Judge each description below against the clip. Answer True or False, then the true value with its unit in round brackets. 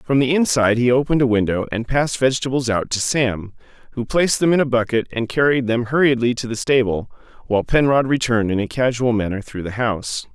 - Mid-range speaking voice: False (120 Hz)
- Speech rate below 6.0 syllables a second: False (6.3 syllables/s)